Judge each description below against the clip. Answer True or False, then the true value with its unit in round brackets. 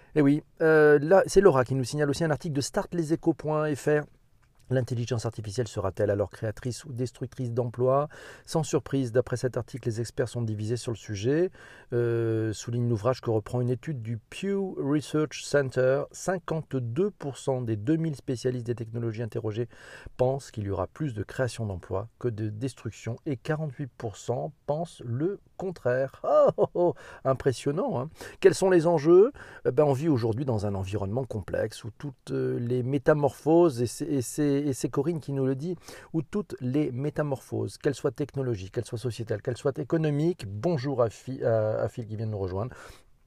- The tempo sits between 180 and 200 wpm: False (170 wpm)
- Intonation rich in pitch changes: False (4.2 semitones)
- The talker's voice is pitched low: True (130 Hz)